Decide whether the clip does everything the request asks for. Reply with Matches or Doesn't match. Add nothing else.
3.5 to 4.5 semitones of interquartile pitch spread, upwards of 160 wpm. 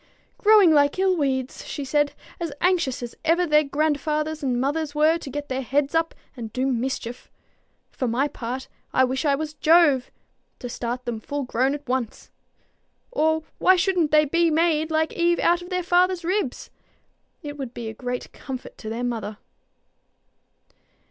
Matches